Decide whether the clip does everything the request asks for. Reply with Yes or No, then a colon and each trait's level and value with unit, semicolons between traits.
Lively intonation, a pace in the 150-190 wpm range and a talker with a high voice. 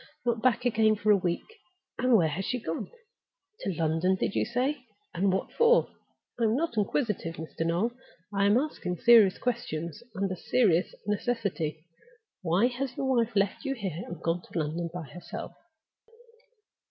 Yes: wide, 5.7 semitones; average, 160 wpm; high, 200 Hz